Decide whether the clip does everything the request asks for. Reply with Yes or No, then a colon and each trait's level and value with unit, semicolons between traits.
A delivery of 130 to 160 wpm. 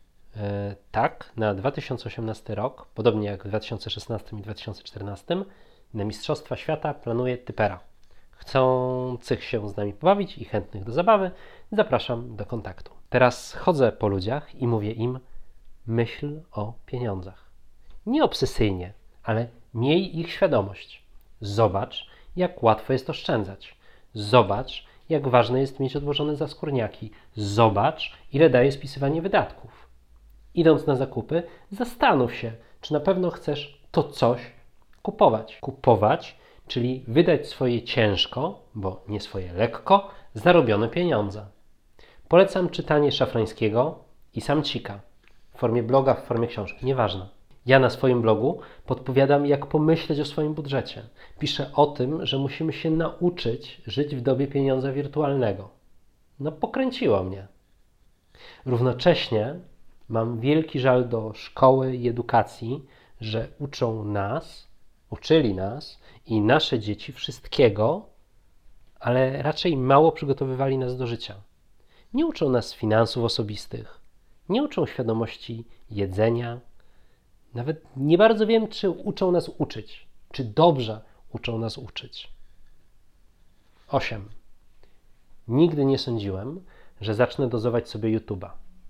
No: average, 120 wpm